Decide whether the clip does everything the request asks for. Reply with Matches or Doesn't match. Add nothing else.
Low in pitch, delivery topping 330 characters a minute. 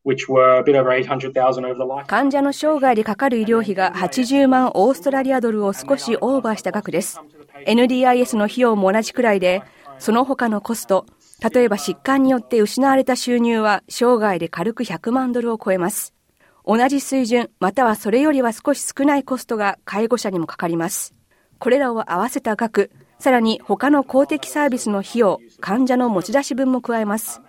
Doesn't match